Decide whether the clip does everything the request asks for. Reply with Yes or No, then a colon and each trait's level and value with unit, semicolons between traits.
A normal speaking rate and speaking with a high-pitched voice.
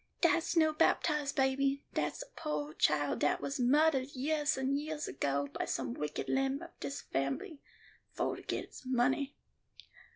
Yes: average, 160 wpm; very high, 270 Hz